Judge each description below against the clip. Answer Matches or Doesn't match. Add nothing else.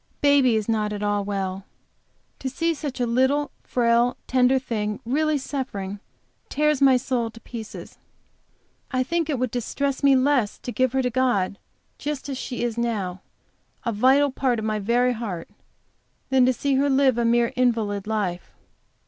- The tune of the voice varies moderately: Matches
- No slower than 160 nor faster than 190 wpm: Matches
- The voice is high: Matches